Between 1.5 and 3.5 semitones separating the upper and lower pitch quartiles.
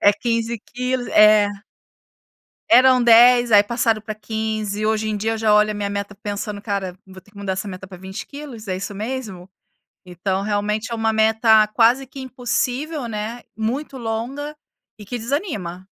Yes: average, 2.9 semitones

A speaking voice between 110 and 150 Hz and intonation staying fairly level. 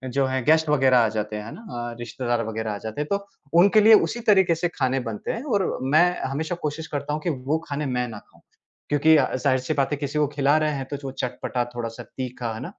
No: medium, 140 Hz; average, 4.2 semitones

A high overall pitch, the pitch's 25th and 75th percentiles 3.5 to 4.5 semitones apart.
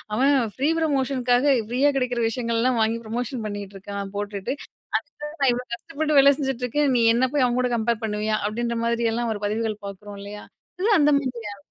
Yes: high, 235 Hz; average, 3.8 semitones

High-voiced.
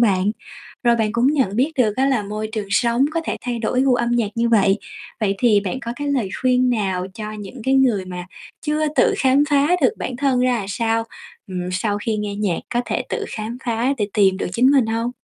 Yes: high, 230 Hz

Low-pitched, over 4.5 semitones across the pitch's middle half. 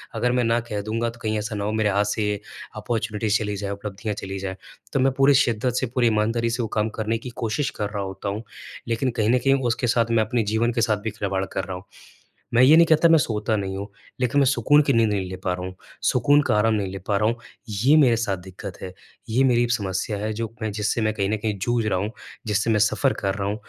No: low, 110 Hz; average, 2.7 semitones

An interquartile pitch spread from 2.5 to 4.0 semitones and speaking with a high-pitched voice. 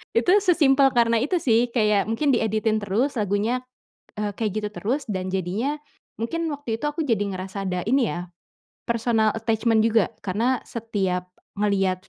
Yes: average, 3.6 semitones; high, 225 Hz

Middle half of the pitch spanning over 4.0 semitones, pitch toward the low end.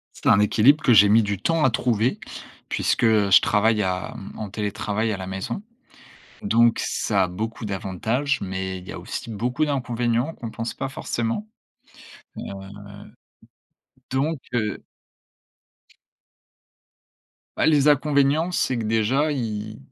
Yes: average, 4.5 semitones; low, 115 Hz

